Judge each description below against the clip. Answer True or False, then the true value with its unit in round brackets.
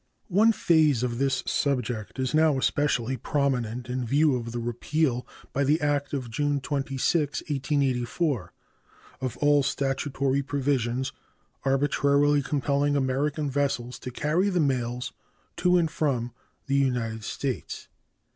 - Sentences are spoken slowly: True (125 wpm)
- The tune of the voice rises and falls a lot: False (2.7 semitones)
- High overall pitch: False (140 Hz)